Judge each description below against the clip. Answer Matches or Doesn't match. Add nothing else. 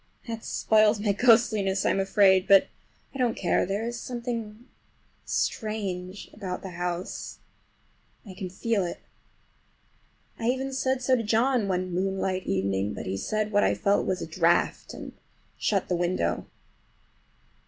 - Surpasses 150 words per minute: Doesn't match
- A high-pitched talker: Matches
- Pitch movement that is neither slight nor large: Matches